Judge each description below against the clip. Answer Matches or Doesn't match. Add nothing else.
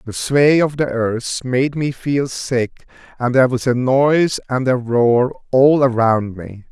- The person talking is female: Doesn't match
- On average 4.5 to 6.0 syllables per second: Doesn't match